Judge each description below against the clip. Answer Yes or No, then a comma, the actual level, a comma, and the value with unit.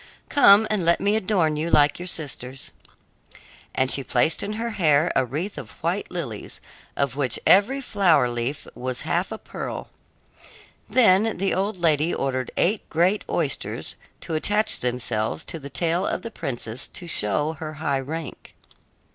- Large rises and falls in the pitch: Yes, wide, 6.3 semitones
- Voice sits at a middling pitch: Yes, medium, 160 Hz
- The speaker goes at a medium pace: Yes, average, 160 wpm